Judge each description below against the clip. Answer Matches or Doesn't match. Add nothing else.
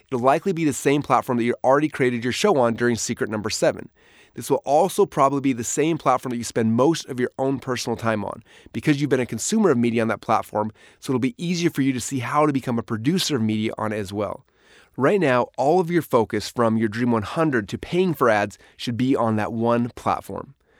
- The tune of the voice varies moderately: Matches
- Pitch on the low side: Matches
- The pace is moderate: Doesn't match